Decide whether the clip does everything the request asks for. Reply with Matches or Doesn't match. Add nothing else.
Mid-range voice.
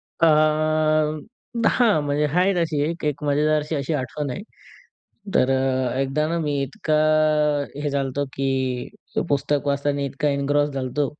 Matches